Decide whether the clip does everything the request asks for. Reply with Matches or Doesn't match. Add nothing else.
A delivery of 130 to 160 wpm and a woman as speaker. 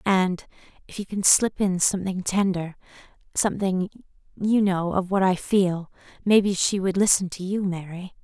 Matches